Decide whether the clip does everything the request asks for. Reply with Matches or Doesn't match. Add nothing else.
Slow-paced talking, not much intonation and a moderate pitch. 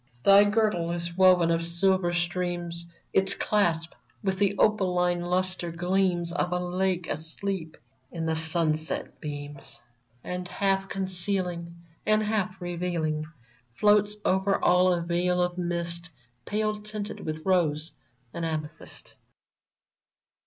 Matches